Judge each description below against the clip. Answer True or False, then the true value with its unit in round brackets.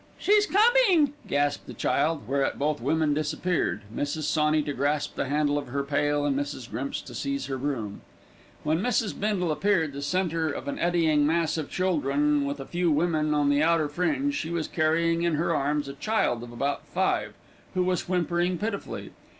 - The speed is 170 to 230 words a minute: True (185 wpm)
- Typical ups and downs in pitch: True (3.5 semitones)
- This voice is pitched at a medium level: True (155 Hz)